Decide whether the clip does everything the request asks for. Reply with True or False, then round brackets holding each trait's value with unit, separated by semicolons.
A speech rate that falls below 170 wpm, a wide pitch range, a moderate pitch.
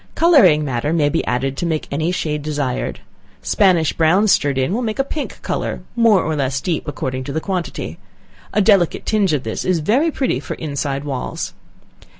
False (185 wpm; 5.9 semitones; 160 Hz)